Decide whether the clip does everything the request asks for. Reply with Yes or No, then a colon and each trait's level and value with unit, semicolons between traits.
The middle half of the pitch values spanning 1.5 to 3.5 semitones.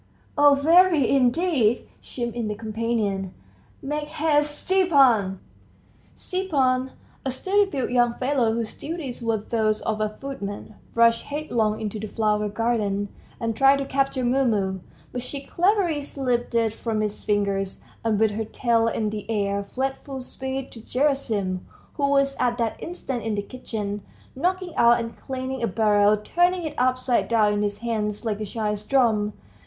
No: average, 4.4 semitones